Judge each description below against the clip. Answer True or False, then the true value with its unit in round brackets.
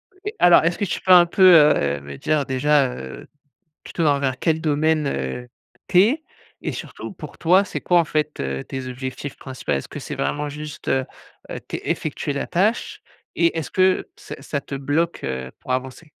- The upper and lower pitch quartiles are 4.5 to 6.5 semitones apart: True (4.8 semitones)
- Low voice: False (150 Hz)